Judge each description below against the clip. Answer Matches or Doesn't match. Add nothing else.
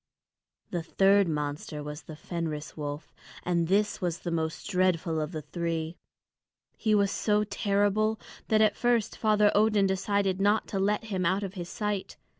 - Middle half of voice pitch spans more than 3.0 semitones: Matches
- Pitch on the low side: Doesn't match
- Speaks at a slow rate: Doesn't match